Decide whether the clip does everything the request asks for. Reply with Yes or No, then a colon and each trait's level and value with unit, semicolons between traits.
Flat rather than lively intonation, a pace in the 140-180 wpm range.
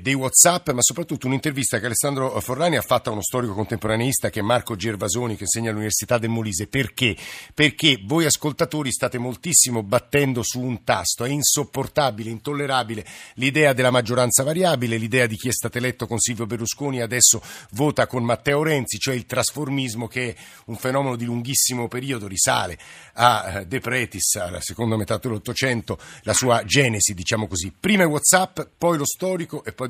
No: average, 3.4 semitones; fast, 170 wpm